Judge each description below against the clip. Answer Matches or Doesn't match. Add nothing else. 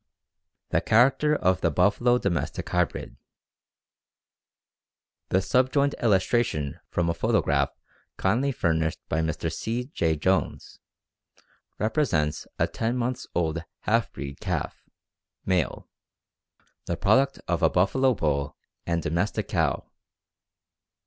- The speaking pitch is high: Doesn't match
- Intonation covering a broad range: Matches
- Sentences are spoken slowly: Matches